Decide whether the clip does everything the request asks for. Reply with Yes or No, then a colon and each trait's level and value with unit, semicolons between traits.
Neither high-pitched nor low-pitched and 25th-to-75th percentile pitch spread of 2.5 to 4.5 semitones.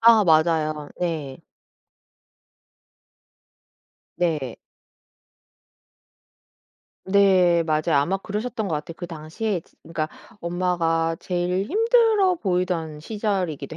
Yes: medium, 175 Hz; average, 4.1 semitones